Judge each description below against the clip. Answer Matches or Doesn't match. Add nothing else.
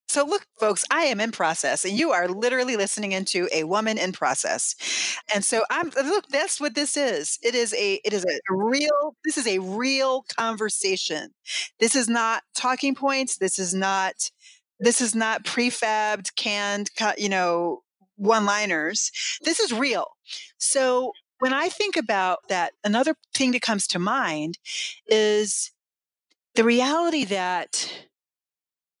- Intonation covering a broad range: Matches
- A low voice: Doesn't match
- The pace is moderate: Matches